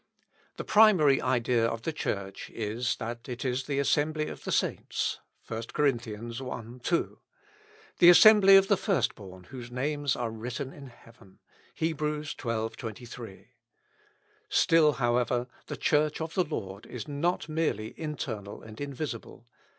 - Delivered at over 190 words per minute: No, average, 145 wpm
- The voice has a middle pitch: No, low, 125 Hz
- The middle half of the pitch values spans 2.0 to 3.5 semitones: No, average, 4.8 semitones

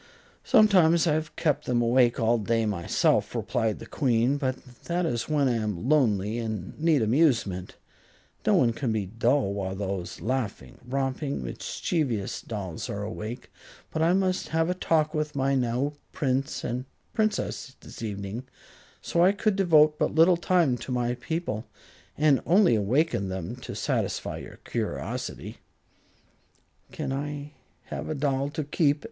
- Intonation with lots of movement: Yes, wide, 5.7 semitones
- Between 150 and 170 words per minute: Yes, average, 155 wpm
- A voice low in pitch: Yes, low, 130 Hz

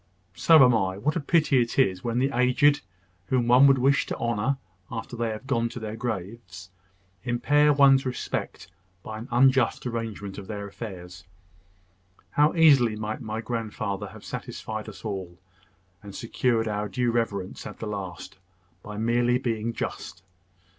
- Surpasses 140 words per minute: Yes, average, 160 wpm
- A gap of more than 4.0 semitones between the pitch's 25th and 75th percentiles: No, average, 3.5 semitones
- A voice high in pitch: No, low, 115 Hz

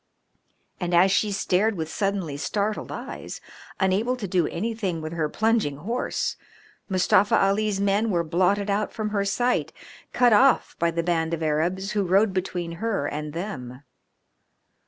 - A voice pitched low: No, high, 190 Hz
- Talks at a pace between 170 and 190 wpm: No, average, 155 wpm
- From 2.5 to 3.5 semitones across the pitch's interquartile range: No, average, 3.9 semitones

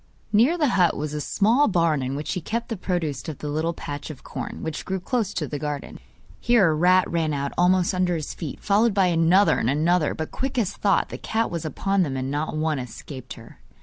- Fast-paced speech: Yes, fast, 230 wpm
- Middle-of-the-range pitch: Yes, medium, 170 Hz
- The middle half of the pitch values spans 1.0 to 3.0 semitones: No, average, 4.8 semitones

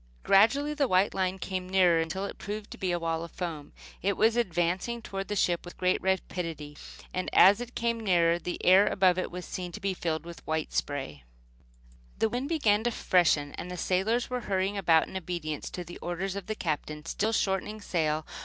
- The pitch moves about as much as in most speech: Yes, average, 3.3 semitones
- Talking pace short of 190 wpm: No, fast, 205 wpm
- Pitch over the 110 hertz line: Yes, medium, 185 Hz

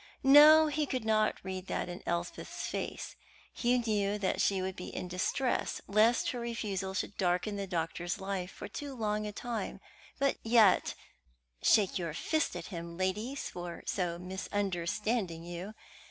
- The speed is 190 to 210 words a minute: No, average, 155 wpm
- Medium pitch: No, high, 200 Hz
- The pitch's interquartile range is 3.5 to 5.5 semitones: Yes, average, 4.0 semitones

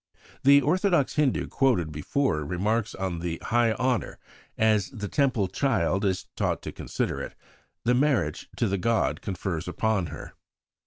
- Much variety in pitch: Yes, wide, 6.5 semitones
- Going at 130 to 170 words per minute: Yes, average, 150 wpm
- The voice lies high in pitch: No, low, 110 Hz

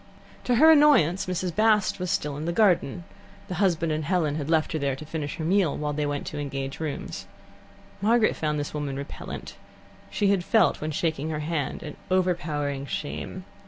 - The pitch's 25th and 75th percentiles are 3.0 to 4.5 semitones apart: Yes, average, 4.1 semitones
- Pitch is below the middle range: No, medium, 160 Hz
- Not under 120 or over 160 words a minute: No, average, 190 wpm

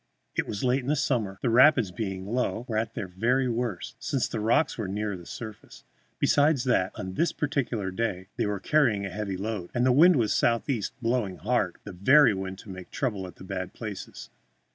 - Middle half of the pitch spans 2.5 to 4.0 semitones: No, average, 4.6 semitones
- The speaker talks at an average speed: No, fast, 210 wpm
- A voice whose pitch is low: Yes, low, 110 Hz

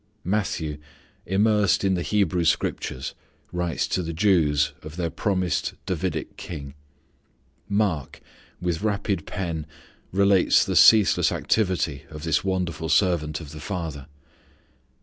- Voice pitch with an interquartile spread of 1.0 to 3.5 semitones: No, average, 3.9 semitones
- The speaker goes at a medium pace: No, slow, 120 wpm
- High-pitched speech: No, very low, 90 Hz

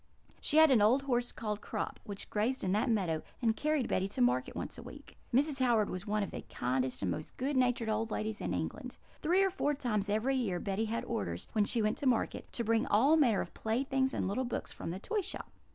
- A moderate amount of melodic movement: Yes, average, 4.5 semitones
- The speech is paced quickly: Yes, fast, 235 wpm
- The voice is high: Yes, high, 225 Hz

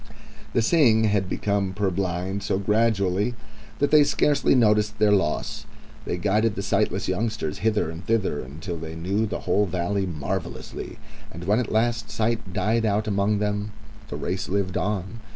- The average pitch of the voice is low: Yes, low, 100 Hz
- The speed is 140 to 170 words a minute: Yes, average, 160 wpm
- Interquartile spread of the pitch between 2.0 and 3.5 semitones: Yes, average, 2.8 semitones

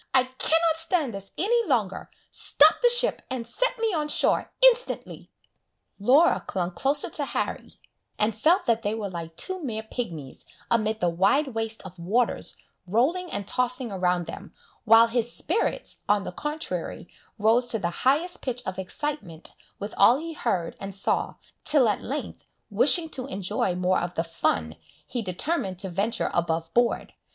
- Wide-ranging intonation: Yes, wide, 7.8 semitones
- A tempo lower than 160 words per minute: No, average, 165 wpm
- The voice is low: No, high, 230 Hz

